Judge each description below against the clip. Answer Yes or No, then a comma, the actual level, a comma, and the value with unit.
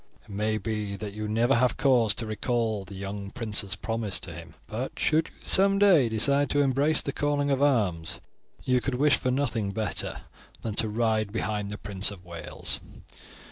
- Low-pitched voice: Yes, low, 110 Hz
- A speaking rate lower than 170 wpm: No, average, 190 wpm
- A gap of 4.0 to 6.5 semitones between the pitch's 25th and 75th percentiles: Yes, average, 4.6 semitones